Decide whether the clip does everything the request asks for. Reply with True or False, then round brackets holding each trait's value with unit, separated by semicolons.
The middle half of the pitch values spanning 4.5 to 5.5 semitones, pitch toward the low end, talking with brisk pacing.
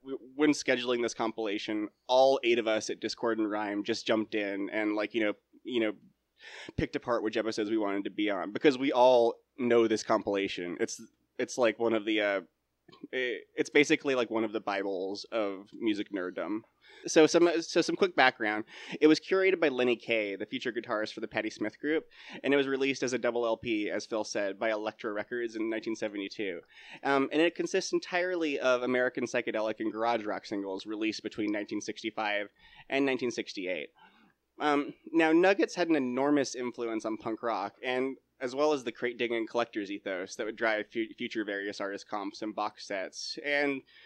False (5.0 semitones; 120 Hz; 185 wpm)